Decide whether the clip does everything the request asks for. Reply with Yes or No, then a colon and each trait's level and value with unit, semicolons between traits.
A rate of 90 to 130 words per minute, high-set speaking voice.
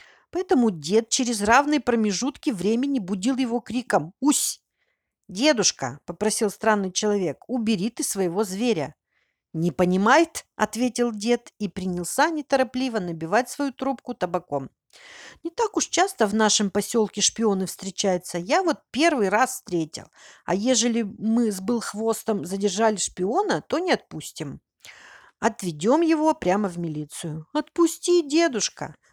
Yes: average, 125 wpm; high, 220 Hz